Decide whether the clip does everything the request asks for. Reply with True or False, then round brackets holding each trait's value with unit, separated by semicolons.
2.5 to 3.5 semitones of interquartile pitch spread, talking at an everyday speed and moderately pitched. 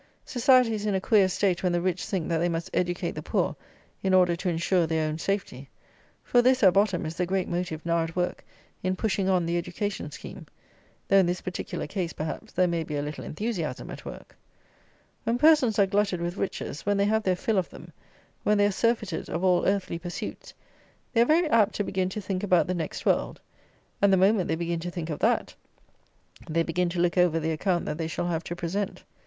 False (3.2 semitones; 225 wpm; 180 Hz)